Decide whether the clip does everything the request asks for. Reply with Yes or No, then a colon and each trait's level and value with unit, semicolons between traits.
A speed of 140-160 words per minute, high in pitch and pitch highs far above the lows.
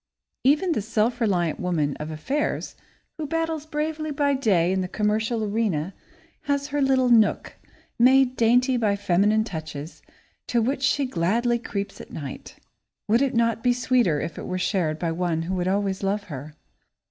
No: average, 170 wpm; high, 220 Hz; wide, 6.3 semitones